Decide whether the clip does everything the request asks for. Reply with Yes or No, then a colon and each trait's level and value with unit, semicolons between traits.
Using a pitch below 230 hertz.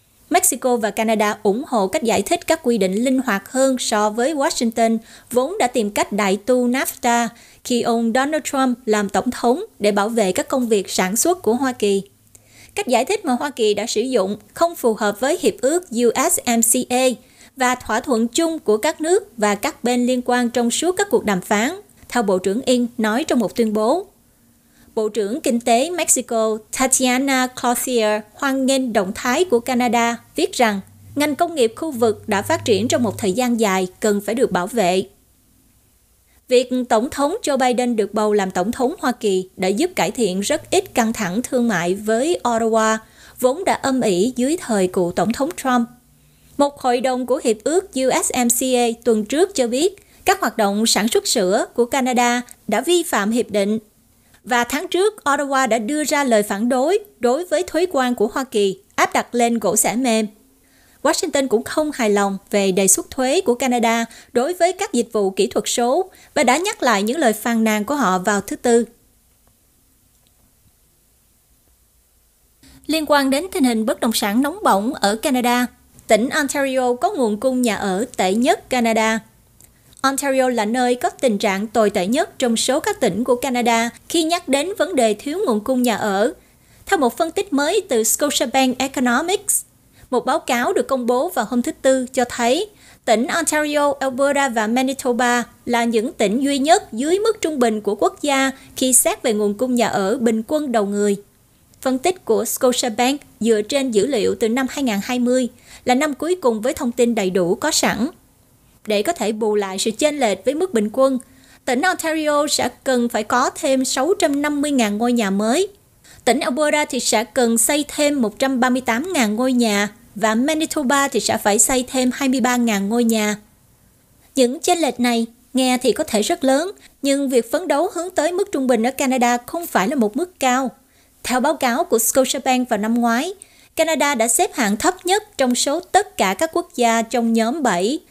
No: high, 245 Hz